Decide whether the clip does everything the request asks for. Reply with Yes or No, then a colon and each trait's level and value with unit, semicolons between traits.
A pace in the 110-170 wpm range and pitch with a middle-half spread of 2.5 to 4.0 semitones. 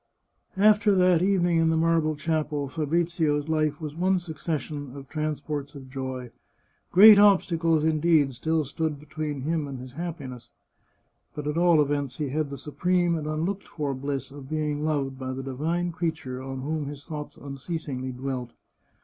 Yes: average, 160 wpm; average, 3.2 semitones